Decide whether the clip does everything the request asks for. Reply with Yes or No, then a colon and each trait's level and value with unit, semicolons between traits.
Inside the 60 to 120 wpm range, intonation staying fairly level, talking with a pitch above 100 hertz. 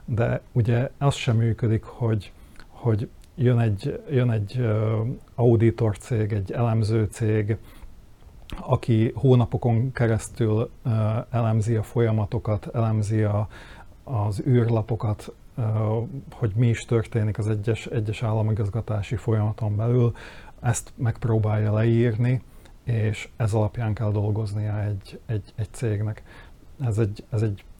Yes: average, 110 wpm; narrow, 1.7 semitones; low, 110 Hz